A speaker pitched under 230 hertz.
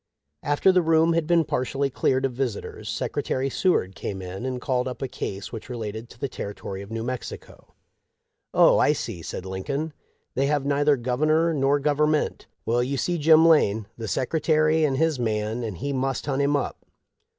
Yes: low, 135 Hz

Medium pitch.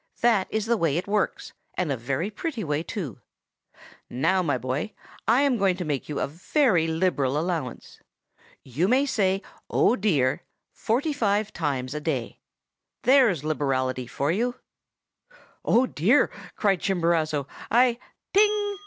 Yes: medium, 180 Hz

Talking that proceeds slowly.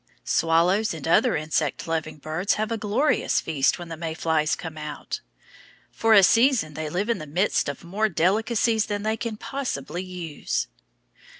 No: average, 170 wpm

